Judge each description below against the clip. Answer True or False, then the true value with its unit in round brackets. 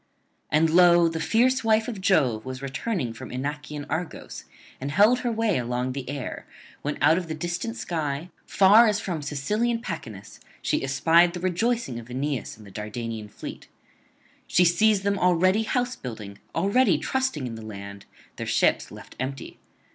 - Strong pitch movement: True (7.6 semitones)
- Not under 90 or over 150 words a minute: False (165 wpm)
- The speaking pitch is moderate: True (160 Hz)